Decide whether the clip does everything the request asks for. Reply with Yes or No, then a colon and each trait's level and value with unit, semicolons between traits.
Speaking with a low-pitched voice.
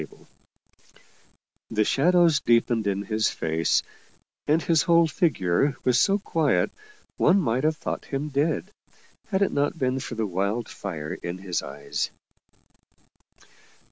Yes: low, 130 Hz